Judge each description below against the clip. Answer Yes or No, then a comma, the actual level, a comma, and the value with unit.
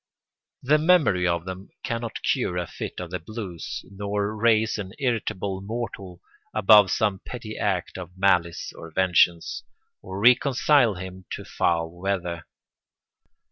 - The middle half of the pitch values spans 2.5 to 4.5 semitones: Yes, average, 3.8 semitones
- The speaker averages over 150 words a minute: No, slow, 135 wpm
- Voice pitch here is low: Yes, very low, 95 Hz